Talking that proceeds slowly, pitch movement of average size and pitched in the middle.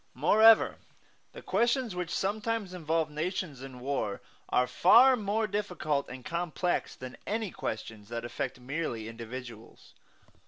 No: slow, 125 wpm; wide, 8.4 semitones; medium, 160 Hz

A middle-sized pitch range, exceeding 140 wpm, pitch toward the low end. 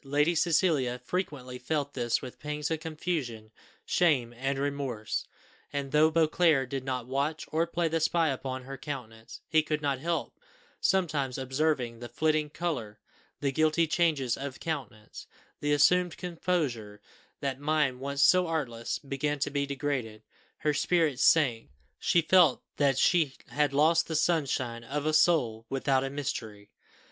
No: average, 3.6 semitones; average, 150 wpm; medium, 145 Hz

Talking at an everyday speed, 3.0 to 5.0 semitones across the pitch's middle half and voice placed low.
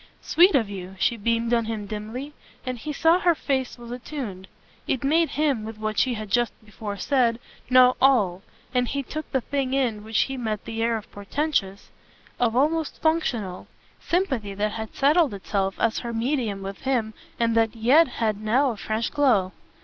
No: average, 185 wpm; average, 4.2 semitones; high, 235 Hz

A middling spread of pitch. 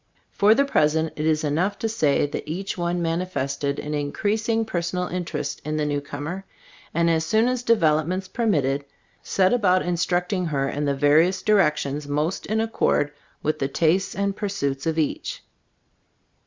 Yes: average, 4.6 semitones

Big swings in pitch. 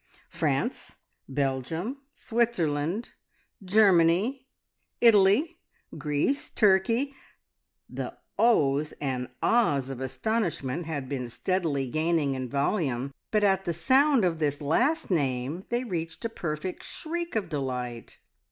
Yes: wide, 8.0 semitones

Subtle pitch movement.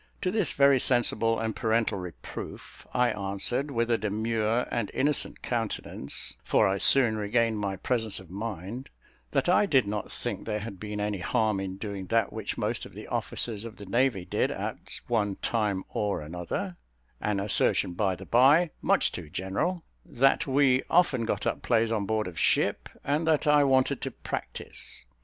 No: average, 4.2 semitones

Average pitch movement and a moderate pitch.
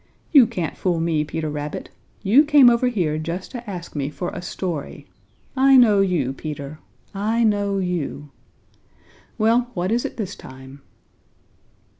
No: wide, 6.7 semitones; medium, 180 Hz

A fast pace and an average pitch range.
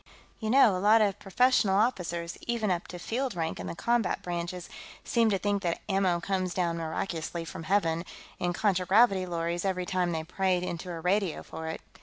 No: average, 190 wpm; average, 3.1 semitones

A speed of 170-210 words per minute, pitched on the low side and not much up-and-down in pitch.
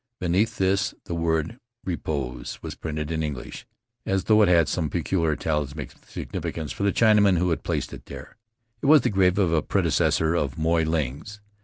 No: average, 180 wpm; very low, 85 Hz; average, 3.7 semitones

